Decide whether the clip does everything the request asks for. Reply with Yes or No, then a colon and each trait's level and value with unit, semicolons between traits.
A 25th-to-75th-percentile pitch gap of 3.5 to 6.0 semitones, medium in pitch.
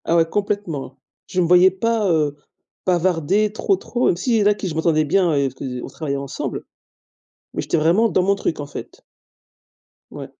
Yes: average, 4.6 semitones; medium, 175 Hz